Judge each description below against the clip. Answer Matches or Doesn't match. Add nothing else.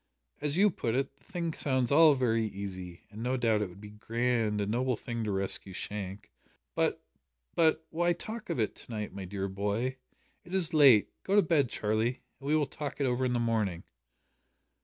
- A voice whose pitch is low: Matches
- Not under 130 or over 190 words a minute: Doesn't match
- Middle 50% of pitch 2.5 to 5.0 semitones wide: Doesn't match